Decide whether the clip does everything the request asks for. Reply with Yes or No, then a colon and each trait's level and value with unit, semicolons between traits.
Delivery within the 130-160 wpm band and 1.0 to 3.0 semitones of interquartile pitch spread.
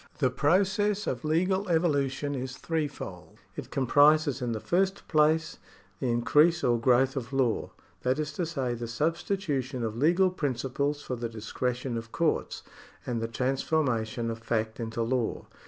No: average, 155 wpm; average, 5.1 semitones